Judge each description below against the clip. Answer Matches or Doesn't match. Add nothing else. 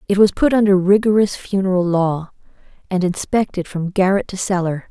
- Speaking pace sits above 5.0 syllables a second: Matches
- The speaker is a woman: Matches